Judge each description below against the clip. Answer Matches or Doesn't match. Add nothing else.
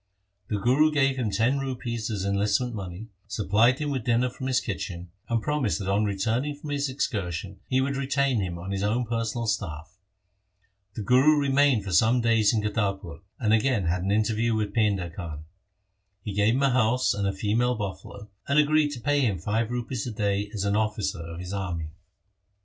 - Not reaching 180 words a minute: Doesn't match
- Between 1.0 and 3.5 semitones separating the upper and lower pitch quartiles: Doesn't match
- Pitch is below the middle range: Matches